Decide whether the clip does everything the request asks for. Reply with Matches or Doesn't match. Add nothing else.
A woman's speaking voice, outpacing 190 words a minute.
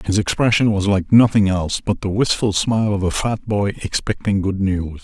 Doesn't match